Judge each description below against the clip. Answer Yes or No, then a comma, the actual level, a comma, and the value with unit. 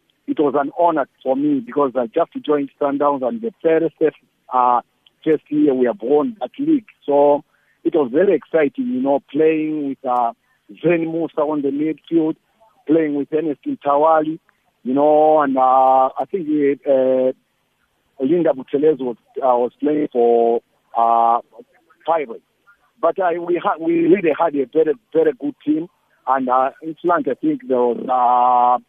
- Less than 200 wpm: Yes, average, 165 wpm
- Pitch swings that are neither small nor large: Yes, average, 4.1 semitones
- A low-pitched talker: No, medium, 150 Hz